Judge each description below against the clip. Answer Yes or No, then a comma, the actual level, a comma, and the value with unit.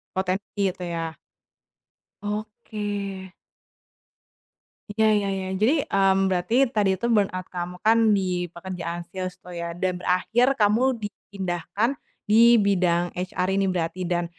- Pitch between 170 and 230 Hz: Yes, high, 190 Hz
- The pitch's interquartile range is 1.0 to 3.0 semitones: Yes, average, 2.7 semitones